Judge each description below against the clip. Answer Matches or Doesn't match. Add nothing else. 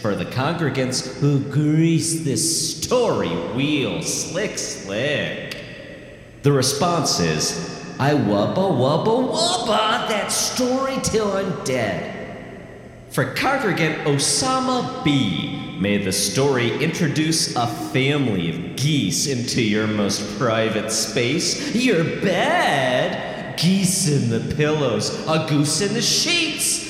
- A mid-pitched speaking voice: Matches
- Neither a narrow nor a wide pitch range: Doesn't match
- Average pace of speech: Doesn't match